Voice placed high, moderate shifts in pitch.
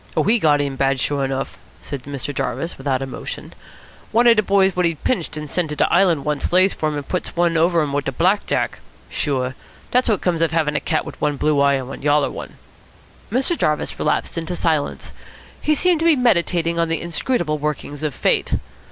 No: medium, 160 Hz; average, 4.1 semitones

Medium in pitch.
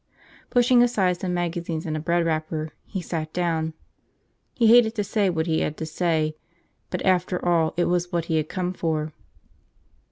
Yes: medium, 170 Hz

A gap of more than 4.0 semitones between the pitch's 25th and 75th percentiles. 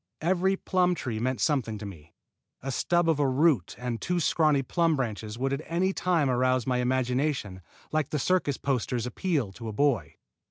Yes: average, 5.2 semitones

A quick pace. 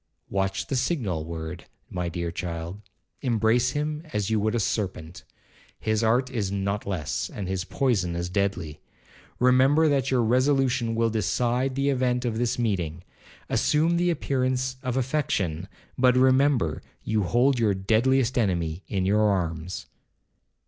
No: average, 140 wpm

